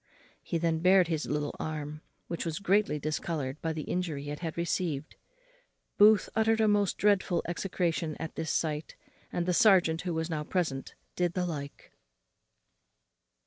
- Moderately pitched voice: Yes, medium, 165 Hz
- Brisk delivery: No, average, 155 wpm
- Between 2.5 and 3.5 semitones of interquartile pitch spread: Yes, average, 3.0 semitones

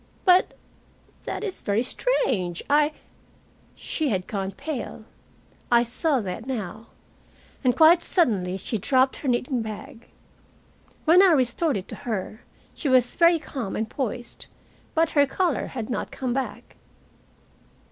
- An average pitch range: No, wide, 5.7 semitones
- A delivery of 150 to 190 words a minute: No, average, 140 wpm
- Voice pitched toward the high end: Yes, very high, 255 Hz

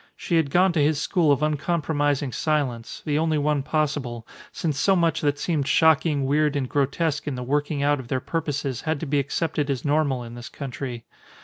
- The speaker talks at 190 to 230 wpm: Yes, average, 200 wpm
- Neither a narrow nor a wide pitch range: No, narrow, 2.3 semitones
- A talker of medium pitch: Yes, medium, 145 Hz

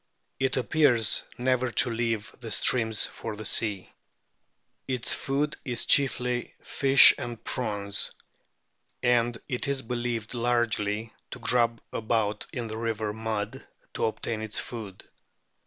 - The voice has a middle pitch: No, low, 115 Hz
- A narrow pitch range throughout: Yes, narrow, 2.1 semitones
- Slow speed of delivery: Yes, slow, 125 wpm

